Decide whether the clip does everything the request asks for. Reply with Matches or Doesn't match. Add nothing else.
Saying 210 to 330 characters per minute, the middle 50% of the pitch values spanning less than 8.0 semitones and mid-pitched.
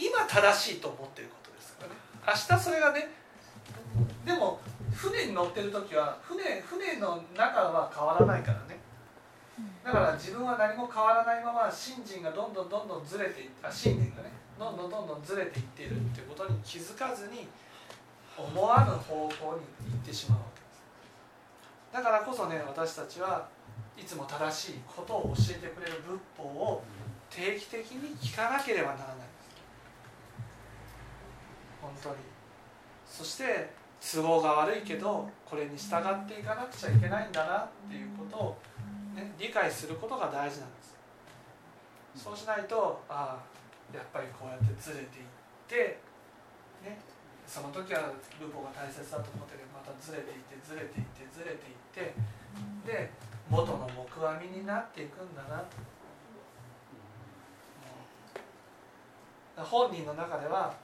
Doesn't match